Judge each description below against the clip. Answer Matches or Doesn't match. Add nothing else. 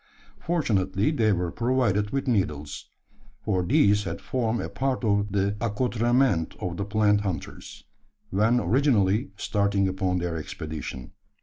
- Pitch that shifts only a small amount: Doesn't match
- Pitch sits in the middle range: Doesn't match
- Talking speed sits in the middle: Doesn't match